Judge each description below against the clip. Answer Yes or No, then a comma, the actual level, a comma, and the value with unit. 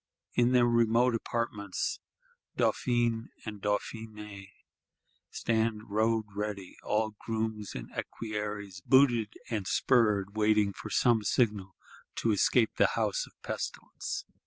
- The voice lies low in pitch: Yes, low, 110 Hz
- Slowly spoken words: Yes, slow, 110 wpm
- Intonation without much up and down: Yes, narrow, 2.1 semitones